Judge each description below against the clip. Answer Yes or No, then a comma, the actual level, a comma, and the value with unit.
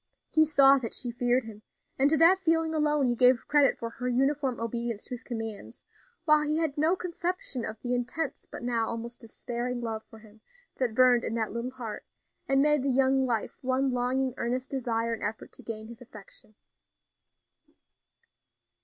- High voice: Yes, very high, 250 Hz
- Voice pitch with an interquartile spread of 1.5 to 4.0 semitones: Yes, average, 3.2 semitones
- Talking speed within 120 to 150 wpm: No, average, 180 wpm